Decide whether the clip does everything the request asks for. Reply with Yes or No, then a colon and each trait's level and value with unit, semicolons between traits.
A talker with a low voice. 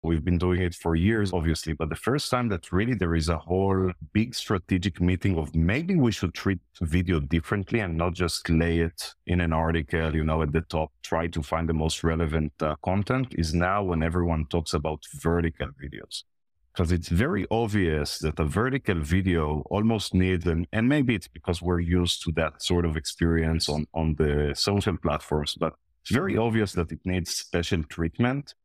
Yes: very low, 85 Hz